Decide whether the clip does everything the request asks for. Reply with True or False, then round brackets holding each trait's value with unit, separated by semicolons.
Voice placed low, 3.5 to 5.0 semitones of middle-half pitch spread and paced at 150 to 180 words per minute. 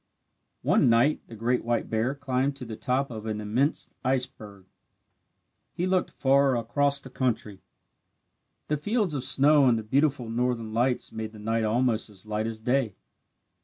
True (125 Hz; 3.8 semitones; 165 wpm)